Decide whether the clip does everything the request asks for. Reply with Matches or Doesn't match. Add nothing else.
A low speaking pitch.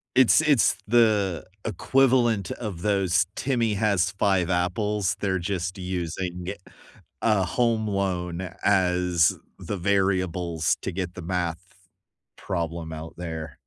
Matches